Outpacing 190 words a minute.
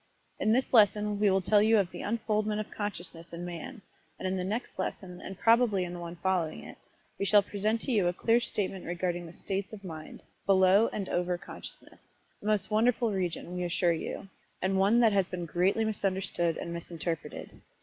Yes: average, 200 wpm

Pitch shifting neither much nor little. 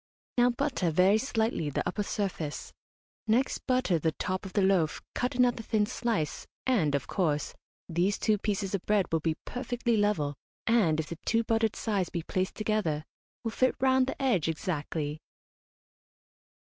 No: wide, 6.0 semitones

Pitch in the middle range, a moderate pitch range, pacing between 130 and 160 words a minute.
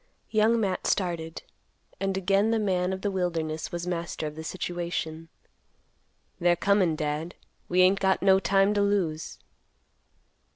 Yes: medium, 180 Hz; average, 3.0 semitones; average, 140 wpm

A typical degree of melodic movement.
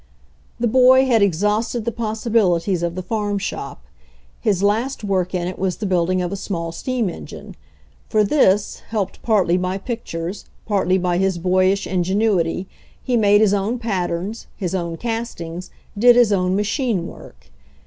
Yes: average, 3.6 semitones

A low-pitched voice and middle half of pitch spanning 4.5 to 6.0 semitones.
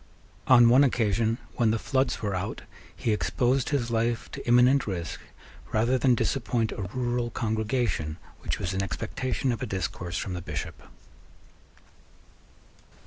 No: low, 115 Hz; average, 3.9 semitones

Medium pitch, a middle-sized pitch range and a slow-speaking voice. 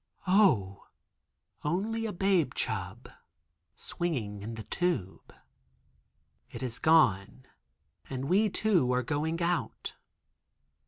No: medium, 150 Hz; wide, 8.2 semitones; slow, 100 wpm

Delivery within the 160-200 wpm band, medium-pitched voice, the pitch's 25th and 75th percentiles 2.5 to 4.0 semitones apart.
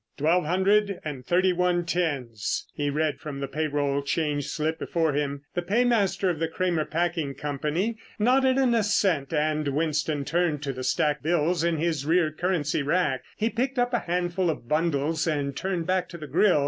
Yes: average, 180 wpm; medium, 160 Hz; average, 3.6 semitones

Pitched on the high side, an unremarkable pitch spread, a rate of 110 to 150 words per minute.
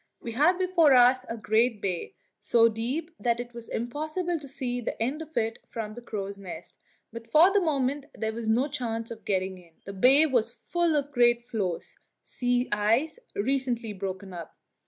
No: high, 240 Hz; average, 4.5 semitones; average, 185 wpm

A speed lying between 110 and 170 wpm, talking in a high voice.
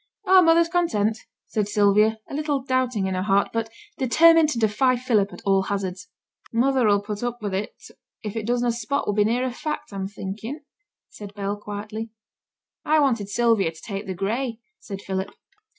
No: average, 180 wpm; high, 220 Hz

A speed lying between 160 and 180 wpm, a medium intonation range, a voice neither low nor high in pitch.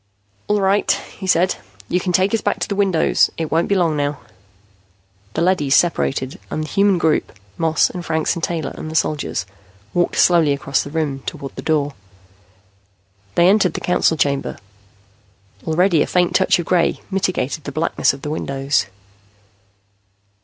Yes: average, 165 wpm; average, 3.7 semitones; medium, 165 Hz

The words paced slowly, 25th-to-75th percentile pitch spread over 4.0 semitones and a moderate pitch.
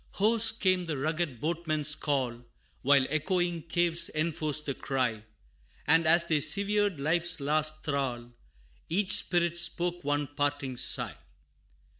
No: slow, 125 wpm; average, 3.3 semitones; medium, 155 Hz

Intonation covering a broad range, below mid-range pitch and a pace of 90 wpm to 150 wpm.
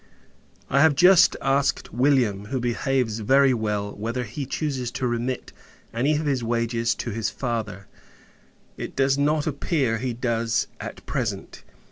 No: average, 3.2 semitones; low, 125 Hz; average, 145 wpm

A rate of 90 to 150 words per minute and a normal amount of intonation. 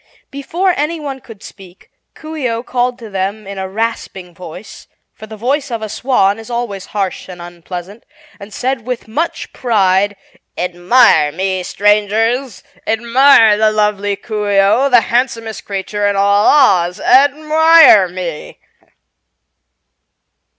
Yes: slow, 135 wpm; average, 4.4 semitones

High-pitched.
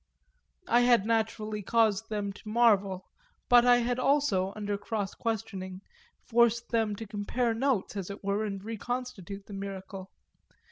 Yes: high, 215 Hz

